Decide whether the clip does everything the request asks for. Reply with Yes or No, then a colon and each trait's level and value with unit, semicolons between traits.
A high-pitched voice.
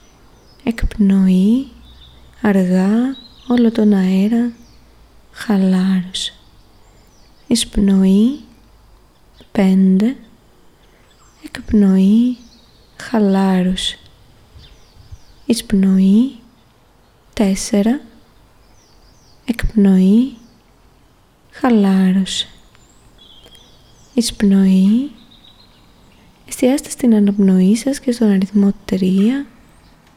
Yes: high, 210 Hz